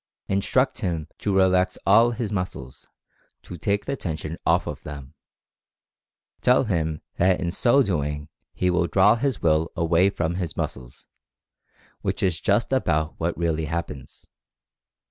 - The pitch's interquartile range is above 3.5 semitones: Yes, average, 4.2 semitones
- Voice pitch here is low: Yes, very low, 90 Hz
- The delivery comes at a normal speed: Yes, average, 150 wpm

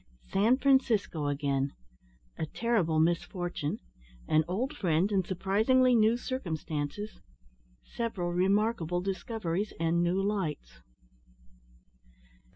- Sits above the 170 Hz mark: Yes, high, 190 Hz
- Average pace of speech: No, slow, 90 wpm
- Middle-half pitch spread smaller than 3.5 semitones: No, average, 5.2 semitones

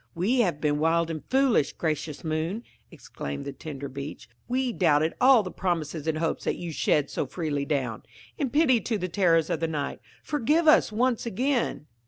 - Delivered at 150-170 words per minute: No, average, 185 wpm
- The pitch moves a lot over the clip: Yes, wide, 7.7 semitones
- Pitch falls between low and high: Yes, medium, 165 Hz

